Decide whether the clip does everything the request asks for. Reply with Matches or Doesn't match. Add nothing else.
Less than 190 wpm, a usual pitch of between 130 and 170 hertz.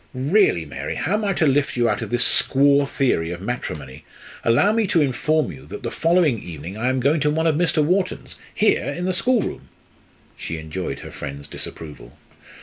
Doesn't match